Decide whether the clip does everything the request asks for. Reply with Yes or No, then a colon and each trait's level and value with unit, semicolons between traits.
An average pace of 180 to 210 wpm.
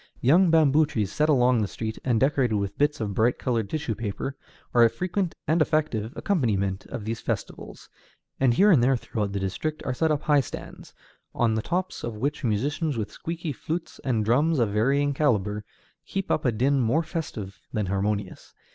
Yes: average, 190 wpm